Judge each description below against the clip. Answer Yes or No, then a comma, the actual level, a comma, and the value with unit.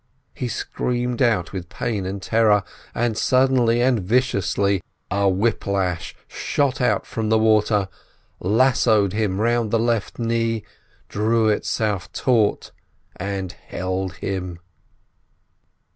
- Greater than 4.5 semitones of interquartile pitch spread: No, average, 3.2 semitones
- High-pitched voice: No, low, 110 Hz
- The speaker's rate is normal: No, slow, 115 wpm